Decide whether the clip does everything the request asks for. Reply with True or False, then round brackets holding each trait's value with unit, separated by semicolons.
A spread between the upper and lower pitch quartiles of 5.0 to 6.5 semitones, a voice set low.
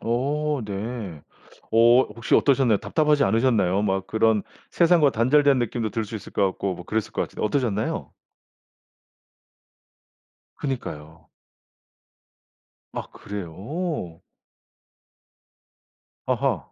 True (5.5 semitones; 115 Hz)